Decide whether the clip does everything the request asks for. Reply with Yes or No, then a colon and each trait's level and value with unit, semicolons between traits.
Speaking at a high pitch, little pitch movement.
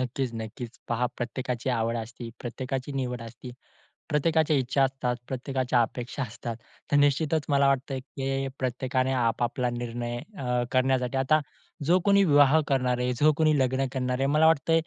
No: low, 130 Hz; narrow, 2.2 semitones